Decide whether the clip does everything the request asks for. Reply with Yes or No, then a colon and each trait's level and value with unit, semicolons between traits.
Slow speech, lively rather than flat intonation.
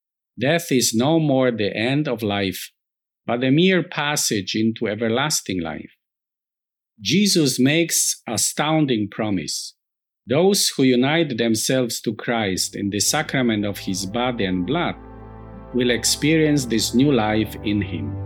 Yes: slow, 130 wpm; wide, 5.7 semitones